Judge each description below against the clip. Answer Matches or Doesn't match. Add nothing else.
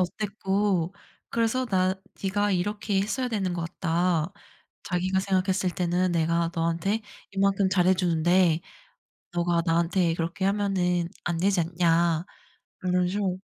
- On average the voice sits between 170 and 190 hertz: Matches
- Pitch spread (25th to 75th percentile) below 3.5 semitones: Matches